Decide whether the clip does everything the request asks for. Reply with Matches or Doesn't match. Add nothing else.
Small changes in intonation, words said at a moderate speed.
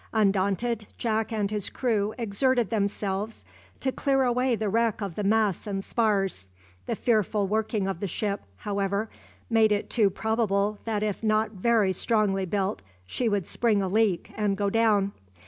Matches